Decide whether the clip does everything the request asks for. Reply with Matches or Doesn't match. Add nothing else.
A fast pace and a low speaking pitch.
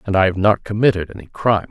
Matches